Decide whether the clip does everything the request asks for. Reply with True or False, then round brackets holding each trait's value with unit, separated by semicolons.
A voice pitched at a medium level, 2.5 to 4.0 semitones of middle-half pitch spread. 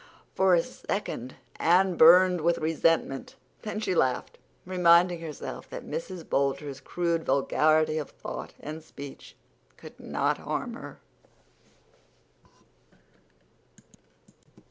True (165 Hz; 2.9 semitones)